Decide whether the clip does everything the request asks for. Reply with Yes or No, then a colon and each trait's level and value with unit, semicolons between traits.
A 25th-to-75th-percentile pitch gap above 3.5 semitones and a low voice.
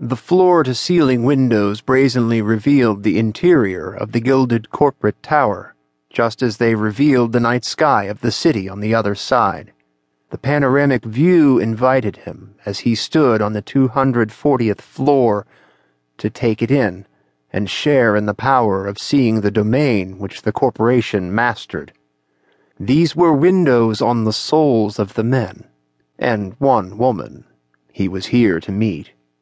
Yes: average, 4.4 semitones; low, 115 Hz